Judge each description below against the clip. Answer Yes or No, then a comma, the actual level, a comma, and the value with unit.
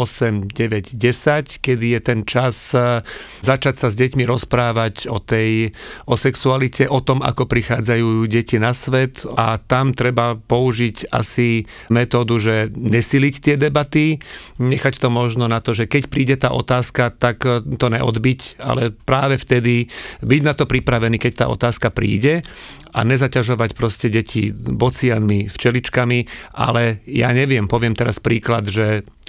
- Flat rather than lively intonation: Yes, narrow, 2.2 semitones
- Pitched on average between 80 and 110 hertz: No, low, 120 Hz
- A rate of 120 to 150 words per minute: Yes, average, 145 wpm